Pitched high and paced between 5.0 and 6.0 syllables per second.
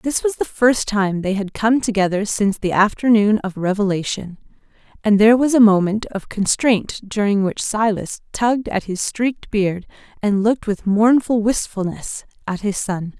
No: high, 210 Hz; 4.7 syllables/s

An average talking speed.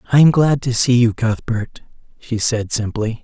Yes: average, 185 wpm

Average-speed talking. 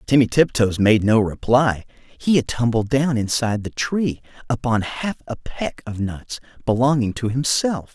Yes: average, 160 wpm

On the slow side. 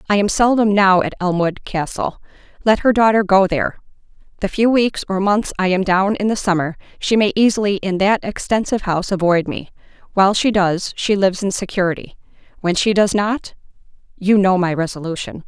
No: average, 170 wpm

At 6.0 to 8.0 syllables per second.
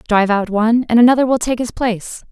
Yes: 6.6 syllables/s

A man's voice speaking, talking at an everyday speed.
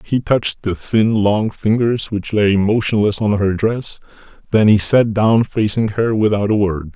Yes: male; average, 180 wpm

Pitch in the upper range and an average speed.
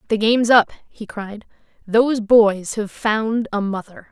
Yes: high, 215 Hz; average, 160 wpm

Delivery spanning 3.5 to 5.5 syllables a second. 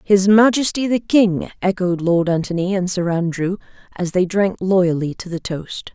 Yes: 4.5 syllables/s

